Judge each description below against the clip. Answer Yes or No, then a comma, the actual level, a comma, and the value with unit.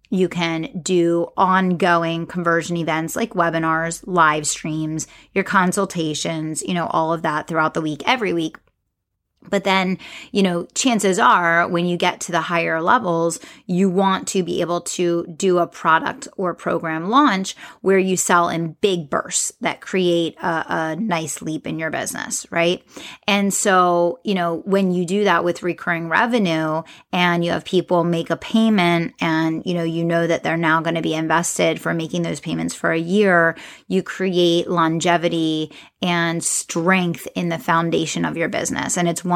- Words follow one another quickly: No, average, 175 wpm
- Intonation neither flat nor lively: No, narrow, 2.2 semitones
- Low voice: No, medium, 170 Hz